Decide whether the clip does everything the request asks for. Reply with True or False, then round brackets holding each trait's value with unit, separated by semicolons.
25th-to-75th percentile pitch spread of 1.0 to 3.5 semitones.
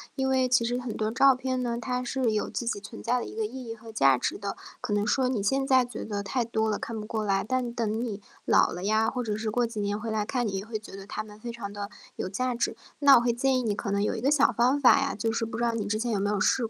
True (3.0 semitones)